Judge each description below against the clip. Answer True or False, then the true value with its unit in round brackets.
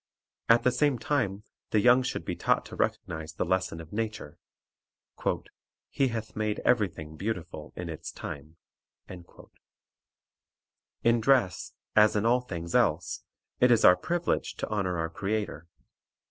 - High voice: False (105 Hz)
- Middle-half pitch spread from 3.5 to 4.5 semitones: False (5.6 semitones)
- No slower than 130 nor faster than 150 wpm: True (145 wpm)